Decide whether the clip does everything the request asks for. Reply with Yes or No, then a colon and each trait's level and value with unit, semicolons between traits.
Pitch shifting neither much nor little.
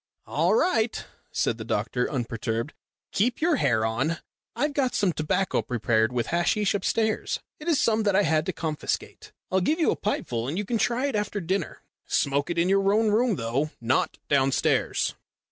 No: wide, 8.8 semitones